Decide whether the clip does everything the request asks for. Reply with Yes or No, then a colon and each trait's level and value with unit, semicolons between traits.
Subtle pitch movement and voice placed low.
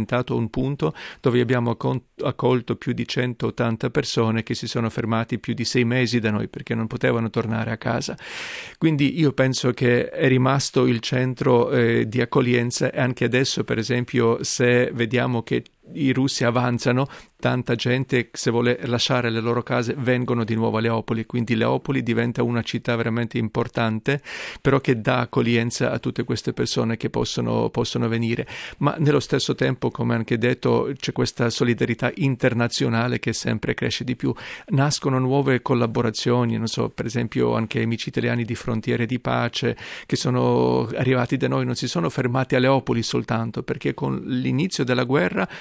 Yes: narrow, 2.0 semitones; low, 120 Hz